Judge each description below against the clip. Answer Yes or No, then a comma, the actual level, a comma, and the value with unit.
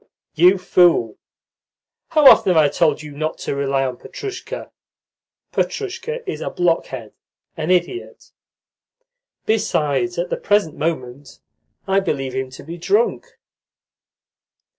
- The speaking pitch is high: No, medium, 170 Hz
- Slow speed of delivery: Yes, slow, 120 wpm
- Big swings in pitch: Yes, wide, 6.4 semitones